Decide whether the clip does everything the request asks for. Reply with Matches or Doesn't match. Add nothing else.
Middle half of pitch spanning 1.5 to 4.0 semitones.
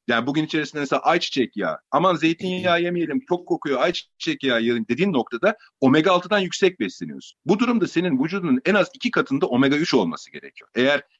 Doesn't match